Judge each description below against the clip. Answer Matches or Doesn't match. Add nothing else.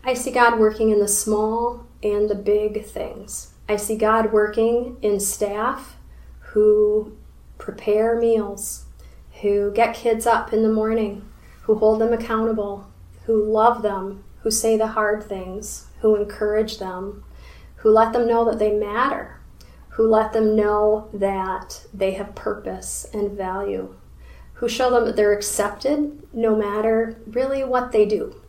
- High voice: Matches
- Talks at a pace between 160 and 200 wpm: Doesn't match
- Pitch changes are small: Matches